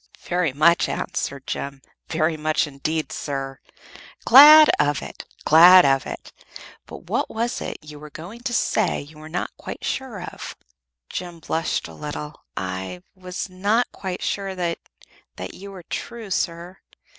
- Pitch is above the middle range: No, medium, 170 Hz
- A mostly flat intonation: No, average, 4.2 semitones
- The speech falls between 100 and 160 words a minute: Yes, average, 155 wpm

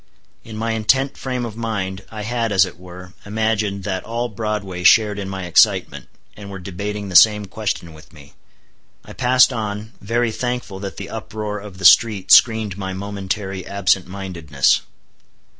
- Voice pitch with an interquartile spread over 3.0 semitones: No, average, 2.7 semitones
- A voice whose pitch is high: No, low, 100 Hz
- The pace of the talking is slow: No, average, 165 wpm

